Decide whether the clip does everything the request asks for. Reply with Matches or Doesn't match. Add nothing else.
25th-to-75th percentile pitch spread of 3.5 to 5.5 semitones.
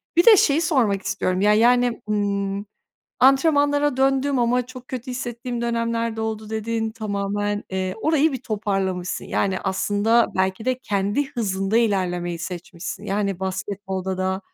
Matches